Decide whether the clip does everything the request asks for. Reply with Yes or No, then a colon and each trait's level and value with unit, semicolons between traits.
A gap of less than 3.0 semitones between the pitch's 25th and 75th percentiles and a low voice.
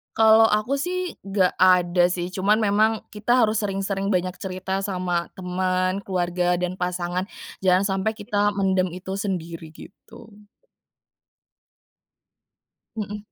No: narrow, 2.5 semitones; high, 190 Hz